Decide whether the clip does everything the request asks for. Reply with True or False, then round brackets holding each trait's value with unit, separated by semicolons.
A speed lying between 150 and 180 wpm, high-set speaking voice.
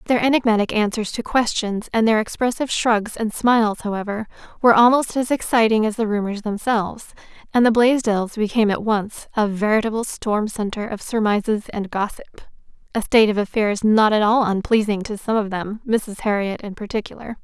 True (170 wpm; 220 Hz)